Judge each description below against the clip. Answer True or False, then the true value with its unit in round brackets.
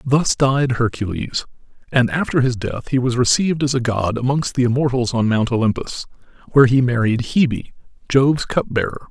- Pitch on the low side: True (125 Hz)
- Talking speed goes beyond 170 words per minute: False (165 wpm)